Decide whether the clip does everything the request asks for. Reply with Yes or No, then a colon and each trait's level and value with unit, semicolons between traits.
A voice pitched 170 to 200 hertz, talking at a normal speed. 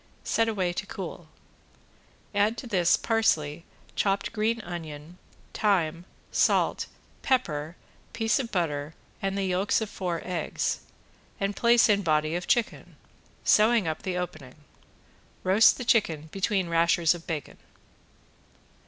No: medium, 185 Hz; slow, 125 wpm